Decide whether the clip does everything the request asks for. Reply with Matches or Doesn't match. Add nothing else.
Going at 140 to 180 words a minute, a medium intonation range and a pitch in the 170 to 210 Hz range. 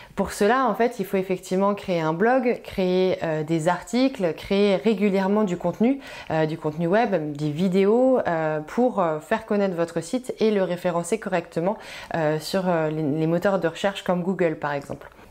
Matches